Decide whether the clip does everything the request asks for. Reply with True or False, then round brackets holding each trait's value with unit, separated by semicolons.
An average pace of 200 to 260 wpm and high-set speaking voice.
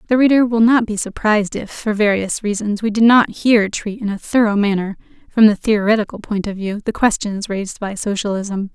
True (205 wpm; 210 Hz)